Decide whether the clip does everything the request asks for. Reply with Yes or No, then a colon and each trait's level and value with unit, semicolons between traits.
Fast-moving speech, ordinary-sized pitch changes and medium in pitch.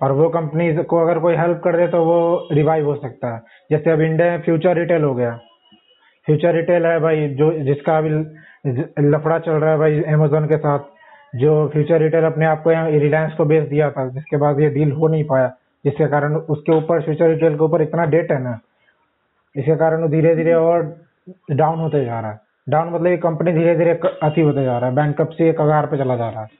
No: fast, 220 wpm; narrow, 2.0 semitones; medium, 155 Hz